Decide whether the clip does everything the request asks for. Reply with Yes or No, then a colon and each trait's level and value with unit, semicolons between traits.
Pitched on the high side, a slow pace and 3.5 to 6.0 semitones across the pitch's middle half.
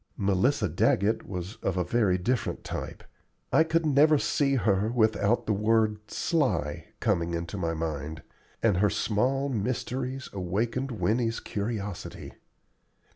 No: low, 105 Hz; slow, 130 wpm; average, 5.3 semitones